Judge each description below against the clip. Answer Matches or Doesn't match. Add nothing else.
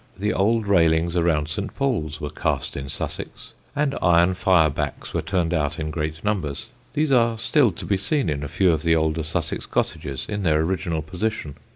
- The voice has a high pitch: Doesn't match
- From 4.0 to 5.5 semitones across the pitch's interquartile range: Matches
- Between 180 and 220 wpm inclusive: Matches